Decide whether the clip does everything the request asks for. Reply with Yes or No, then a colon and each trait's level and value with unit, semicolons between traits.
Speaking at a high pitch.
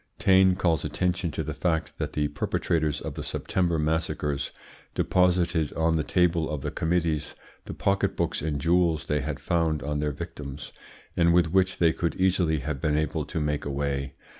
No: very low, 80 Hz